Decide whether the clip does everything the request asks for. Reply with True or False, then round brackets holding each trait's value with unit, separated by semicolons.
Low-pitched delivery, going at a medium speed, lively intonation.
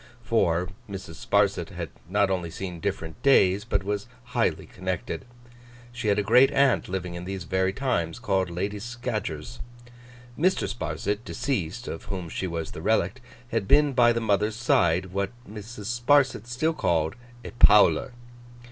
False (100 Hz; 155 wpm; 5.0 semitones)